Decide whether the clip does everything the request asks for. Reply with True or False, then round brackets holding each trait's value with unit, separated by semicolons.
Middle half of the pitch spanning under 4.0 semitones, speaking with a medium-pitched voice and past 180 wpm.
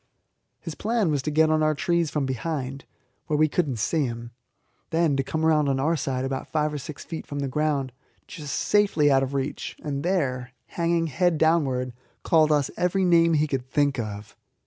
True (3.3 semitones; 150 Hz; 200 wpm)